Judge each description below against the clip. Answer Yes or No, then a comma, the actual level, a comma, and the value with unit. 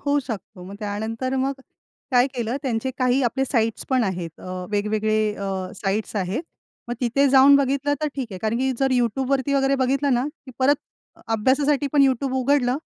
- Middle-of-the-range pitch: No, very high, 255 Hz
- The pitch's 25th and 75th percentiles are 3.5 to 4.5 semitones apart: Yes, average, 3.9 semitones